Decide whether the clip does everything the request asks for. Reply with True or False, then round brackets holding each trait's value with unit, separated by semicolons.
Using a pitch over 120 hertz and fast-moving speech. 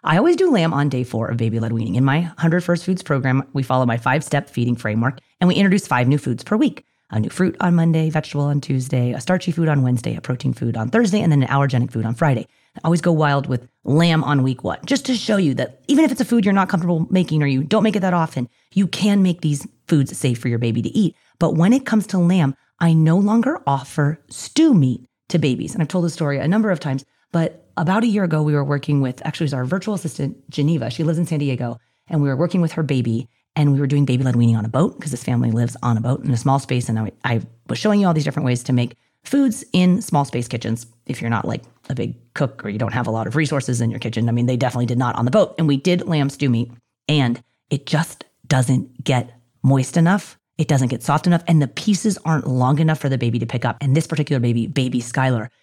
True (140 Hz; 270 wpm)